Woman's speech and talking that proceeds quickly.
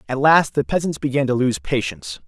No: male; fast, 210 wpm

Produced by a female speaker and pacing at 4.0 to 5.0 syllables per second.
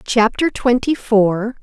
No: female; 3.4 syllables/s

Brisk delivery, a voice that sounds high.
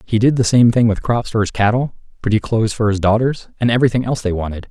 No: fast, 255 wpm; low, 110 Hz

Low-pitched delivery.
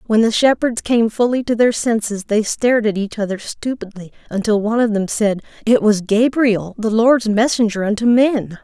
No: high, 220 Hz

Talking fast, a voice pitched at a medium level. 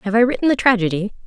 No: fast, 240 wpm; high, 220 Hz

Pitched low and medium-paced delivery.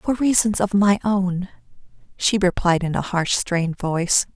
No: high, 190 Hz; average, 165 wpm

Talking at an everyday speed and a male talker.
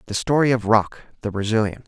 Yes: average, 190 wpm; male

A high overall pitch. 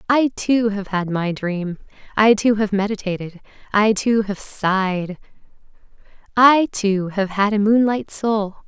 Yes: high, 205 Hz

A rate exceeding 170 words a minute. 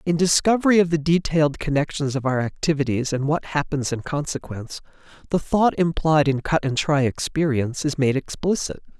No: average, 165 wpm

